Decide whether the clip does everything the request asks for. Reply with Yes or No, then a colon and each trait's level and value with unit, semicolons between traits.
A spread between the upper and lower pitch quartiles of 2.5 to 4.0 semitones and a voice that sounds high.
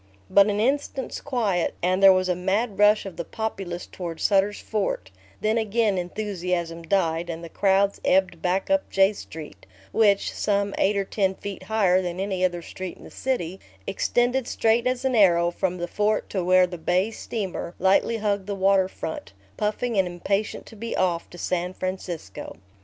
Yes: average, 3.0 semitones; high, 195 Hz